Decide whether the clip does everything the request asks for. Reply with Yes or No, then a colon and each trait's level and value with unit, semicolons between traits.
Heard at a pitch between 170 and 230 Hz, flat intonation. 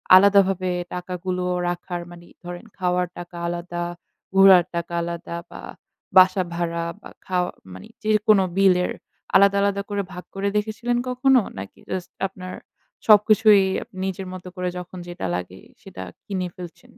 Yes: medium, 185 Hz; narrow, 2.3 semitones